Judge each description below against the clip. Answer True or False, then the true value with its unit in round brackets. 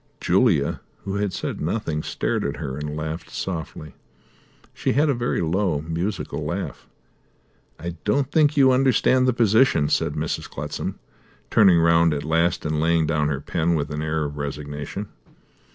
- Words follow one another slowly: False (160 wpm)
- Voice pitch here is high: False (85 Hz)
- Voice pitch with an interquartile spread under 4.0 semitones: False (5.4 semitones)